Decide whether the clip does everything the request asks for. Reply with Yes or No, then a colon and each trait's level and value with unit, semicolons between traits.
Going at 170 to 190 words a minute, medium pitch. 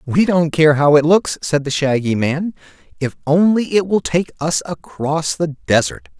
Yes: average, 185 wpm; medium, 155 Hz